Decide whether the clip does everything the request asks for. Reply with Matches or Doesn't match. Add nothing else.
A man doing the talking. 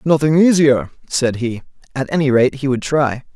Matches